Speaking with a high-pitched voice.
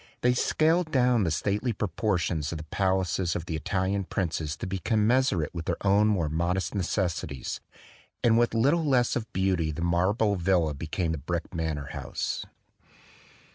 No: very low, 95 Hz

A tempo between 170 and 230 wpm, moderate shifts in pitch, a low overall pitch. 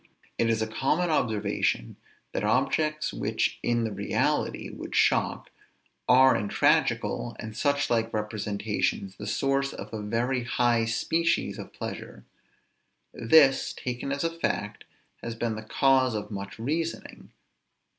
No: slow, 135 wpm; average, 4.0 semitones; low, 115 Hz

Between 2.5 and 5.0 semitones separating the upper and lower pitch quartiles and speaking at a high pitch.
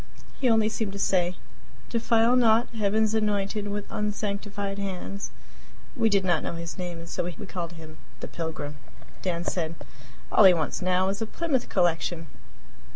Yes: average, 3.7 semitones; high, 200 Hz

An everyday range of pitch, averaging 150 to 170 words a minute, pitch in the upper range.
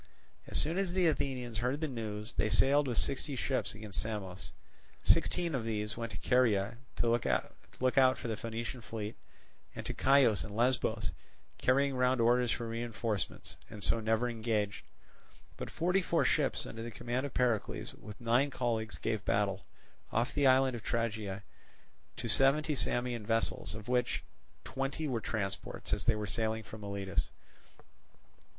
No: average, 3.2 semitones; average, 160 wpm; low, 115 Hz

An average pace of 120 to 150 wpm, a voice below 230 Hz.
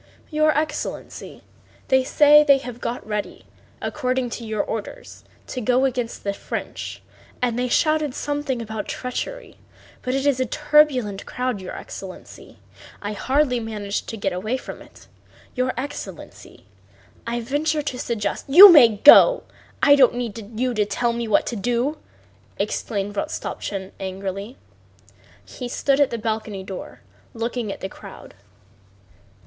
No: average, 145 wpm; high, 245 Hz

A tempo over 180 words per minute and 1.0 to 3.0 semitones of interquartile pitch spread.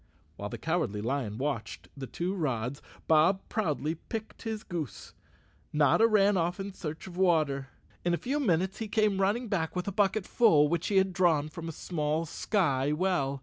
No: average, 190 wpm; average, 4.9 semitones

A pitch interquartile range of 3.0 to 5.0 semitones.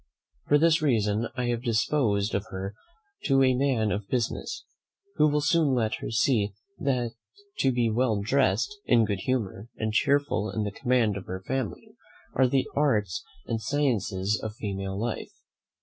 Yes: average, 4.4 semitones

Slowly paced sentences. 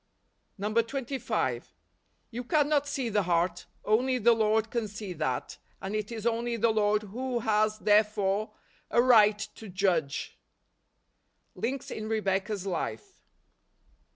Yes: slow, 125 wpm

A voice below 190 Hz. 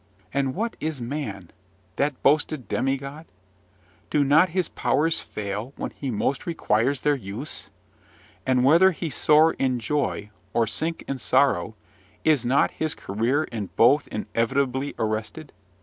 Yes: low, 135 Hz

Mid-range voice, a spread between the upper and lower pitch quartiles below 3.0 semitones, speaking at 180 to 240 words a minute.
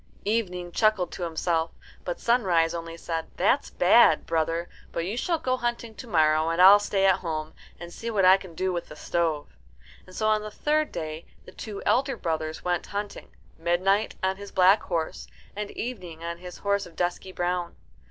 No: medium, 180 Hz; average, 3.8 semitones; average, 190 wpm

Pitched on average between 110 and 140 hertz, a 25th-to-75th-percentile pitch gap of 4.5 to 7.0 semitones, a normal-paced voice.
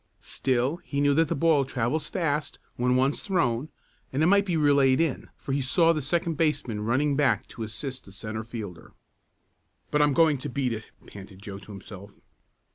Yes: low, 135 Hz; average, 4.9 semitones; average, 190 wpm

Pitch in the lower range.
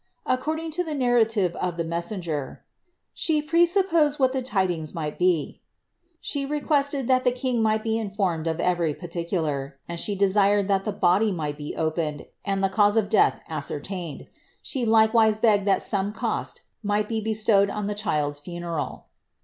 No: high, 205 Hz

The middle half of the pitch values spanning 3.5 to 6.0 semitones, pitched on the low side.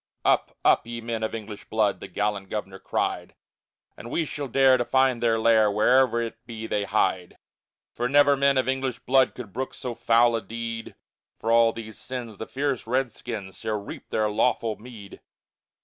No: average, 2.8 semitones; low, 115 Hz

